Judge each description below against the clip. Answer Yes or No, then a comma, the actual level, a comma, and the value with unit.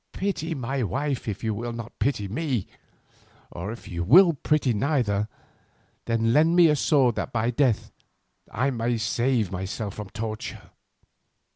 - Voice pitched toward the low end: Yes, low, 120 Hz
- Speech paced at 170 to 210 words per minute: No, average, 150 wpm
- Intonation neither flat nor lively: Yes, average, 4.7 semitones